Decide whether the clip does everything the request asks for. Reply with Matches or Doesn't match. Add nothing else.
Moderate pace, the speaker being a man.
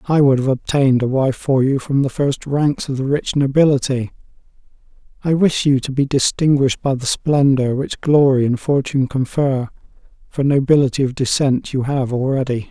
Matches